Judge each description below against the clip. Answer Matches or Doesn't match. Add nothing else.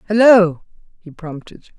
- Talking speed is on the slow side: Matches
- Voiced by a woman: Matches